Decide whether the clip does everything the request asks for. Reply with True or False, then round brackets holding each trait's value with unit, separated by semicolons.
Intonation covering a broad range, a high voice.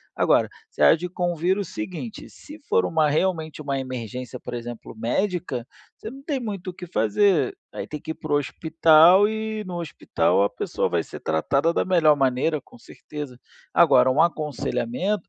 False (5.9 semitones; 160 Hz)